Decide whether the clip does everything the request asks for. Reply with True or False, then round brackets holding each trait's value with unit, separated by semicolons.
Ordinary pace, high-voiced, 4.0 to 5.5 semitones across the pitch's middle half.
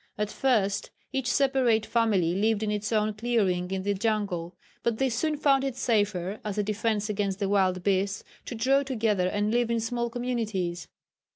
False (180 wpm; 215 Hz; 3.2 semitones)